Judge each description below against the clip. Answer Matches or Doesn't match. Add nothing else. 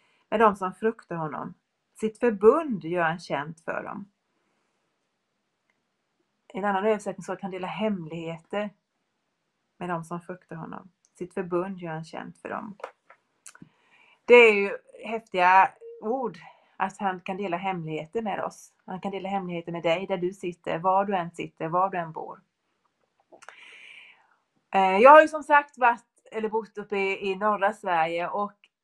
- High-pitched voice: Matches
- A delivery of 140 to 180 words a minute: Matches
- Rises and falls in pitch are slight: Doesn't match